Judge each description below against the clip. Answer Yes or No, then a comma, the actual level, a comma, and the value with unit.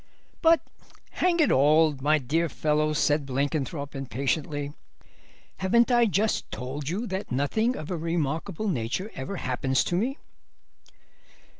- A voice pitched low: No, medium, 155 Hz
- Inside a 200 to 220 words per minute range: No, slow, 135 wpm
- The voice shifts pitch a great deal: Yes, wide, 6.0 semitones